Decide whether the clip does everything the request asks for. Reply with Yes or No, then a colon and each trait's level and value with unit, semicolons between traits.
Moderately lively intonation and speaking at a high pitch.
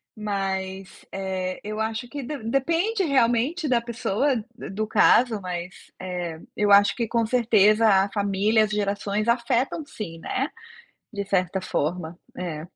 Yes: average, 3.9 semitones; high, 210 Hz